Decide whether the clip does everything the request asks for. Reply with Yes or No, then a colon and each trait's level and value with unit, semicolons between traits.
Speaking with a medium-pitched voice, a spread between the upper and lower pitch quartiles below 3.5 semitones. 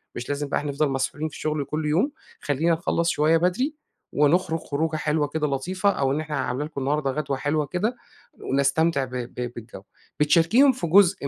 Yes: medium, 150 Hz; average, 3.1 semitones